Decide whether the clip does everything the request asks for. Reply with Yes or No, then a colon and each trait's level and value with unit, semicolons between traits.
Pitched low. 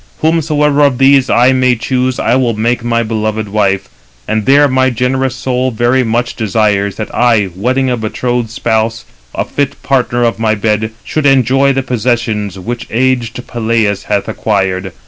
Yes: low, 120 Hz